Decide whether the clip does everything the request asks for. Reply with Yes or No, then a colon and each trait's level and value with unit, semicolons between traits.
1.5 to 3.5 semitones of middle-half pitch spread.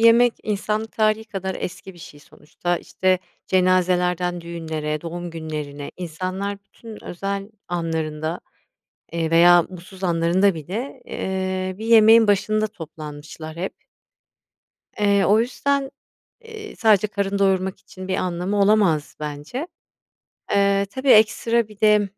No: average, 3.9 semitones